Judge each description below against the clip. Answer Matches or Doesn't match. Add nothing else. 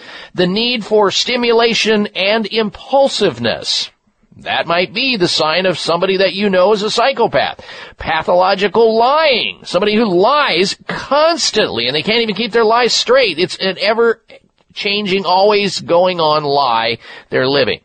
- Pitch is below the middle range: Doesn't match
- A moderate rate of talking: Matches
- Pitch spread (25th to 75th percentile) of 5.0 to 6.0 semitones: Doesn't match